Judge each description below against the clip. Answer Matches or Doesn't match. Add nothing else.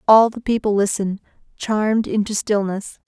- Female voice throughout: Matches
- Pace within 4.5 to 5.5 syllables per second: Matches